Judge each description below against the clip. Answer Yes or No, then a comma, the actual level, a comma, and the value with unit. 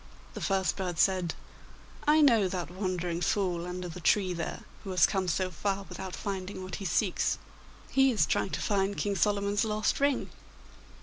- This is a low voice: No, high, 190 Hz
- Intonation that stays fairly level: Yes, narrow, 2.3 semitones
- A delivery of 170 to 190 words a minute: Yes, average, 175 wpm